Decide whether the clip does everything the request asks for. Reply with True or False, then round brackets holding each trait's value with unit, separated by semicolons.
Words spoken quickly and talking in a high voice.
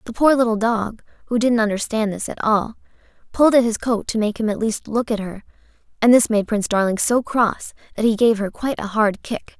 True (230 wpm; 220 Hz)